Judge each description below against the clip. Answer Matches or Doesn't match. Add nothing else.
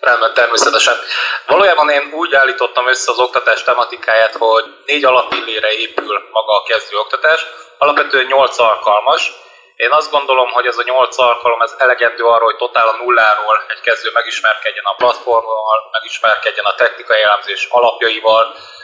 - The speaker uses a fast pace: Doesn't match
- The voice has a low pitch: Matches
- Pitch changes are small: Matches